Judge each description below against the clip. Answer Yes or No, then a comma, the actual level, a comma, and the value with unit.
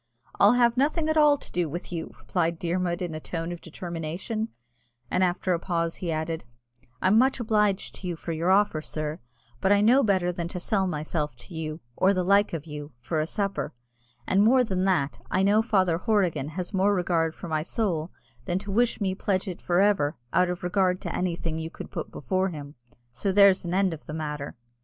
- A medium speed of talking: No, fast, 215 wpm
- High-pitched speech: No, medium, 180 Hz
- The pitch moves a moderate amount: Yes, average, 3.5 semitones